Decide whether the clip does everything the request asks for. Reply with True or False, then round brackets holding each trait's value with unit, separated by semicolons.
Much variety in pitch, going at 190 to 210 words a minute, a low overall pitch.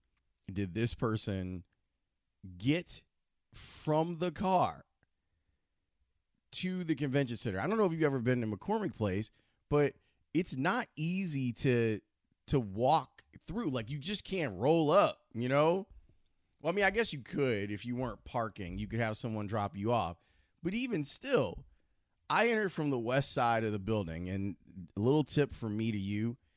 False (7.2 semitones; 170 wpm; 115 Hz)